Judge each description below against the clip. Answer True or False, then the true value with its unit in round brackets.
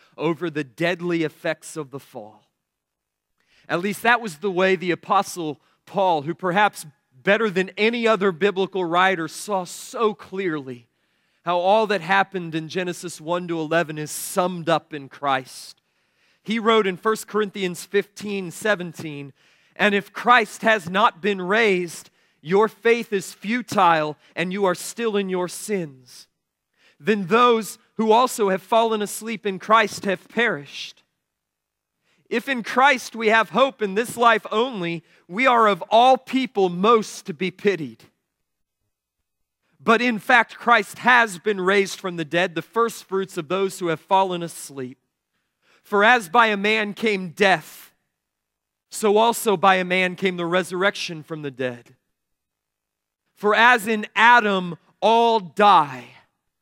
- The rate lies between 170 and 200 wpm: False (145 wpm)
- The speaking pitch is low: False (195 Hz)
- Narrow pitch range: False (4.3 semitones)